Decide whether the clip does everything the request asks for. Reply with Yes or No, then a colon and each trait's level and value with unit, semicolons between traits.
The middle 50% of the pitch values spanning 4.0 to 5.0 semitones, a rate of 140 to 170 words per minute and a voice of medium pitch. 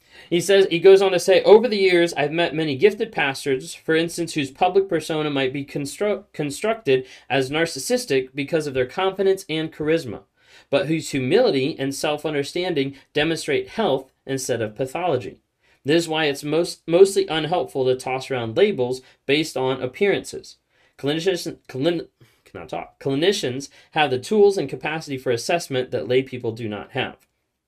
Yes: average, 4.4 semitones; average, 160 wpm; medium, 150 Hz